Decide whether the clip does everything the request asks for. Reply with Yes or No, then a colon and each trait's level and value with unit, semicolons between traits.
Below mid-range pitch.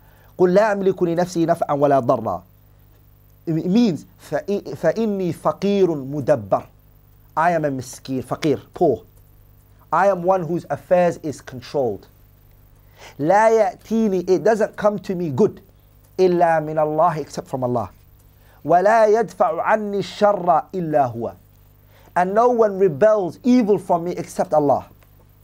No: medium, 155 Hz